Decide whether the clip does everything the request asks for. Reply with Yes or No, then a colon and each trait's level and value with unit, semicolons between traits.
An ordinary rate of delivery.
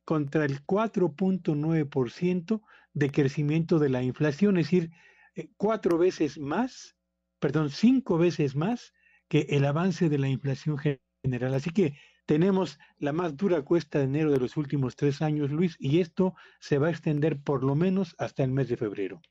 Yes: average, 170 wpm